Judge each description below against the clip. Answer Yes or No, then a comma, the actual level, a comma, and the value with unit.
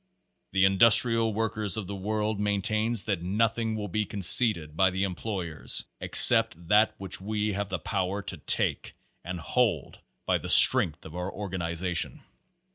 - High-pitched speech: No, low, 100 Hz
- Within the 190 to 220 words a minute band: No, average, 160 wpm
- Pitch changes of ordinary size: Yes, average, 3.1 semitones